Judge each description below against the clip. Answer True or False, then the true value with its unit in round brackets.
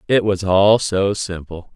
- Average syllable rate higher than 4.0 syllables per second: False (3.8 syllables/s)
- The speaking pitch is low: True (100 Hz)